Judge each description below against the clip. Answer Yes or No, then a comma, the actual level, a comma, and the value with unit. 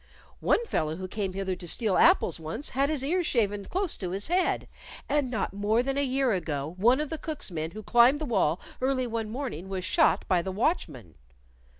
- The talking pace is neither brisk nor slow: No, fast, 210 wpm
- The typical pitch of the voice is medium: No, high, 220 Hz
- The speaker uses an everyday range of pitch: No, wide, 6.7 semitones